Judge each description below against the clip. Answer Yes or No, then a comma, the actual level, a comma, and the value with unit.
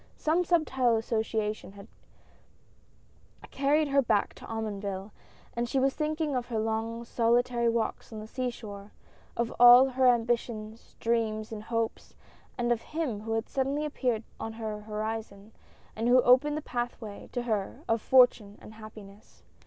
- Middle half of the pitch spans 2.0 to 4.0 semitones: Yes, narrow, 2.6 semitones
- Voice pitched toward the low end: No, high, 230 Hz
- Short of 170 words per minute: Yes, average, 155 wpm